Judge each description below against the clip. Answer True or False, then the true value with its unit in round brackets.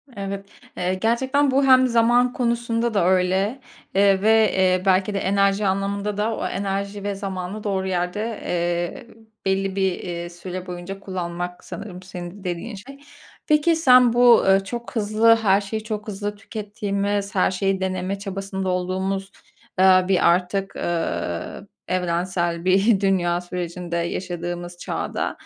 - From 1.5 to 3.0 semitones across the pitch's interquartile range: True (2.5 semitones)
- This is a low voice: False (195 Hz)